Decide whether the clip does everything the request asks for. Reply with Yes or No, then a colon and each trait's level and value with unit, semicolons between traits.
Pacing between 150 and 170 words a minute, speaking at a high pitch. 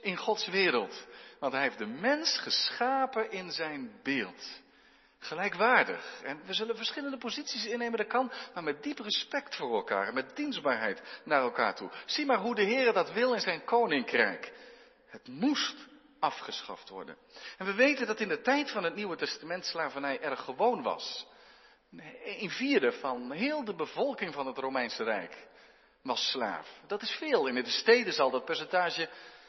Yes: average, 165 wpm; high, 235 Hz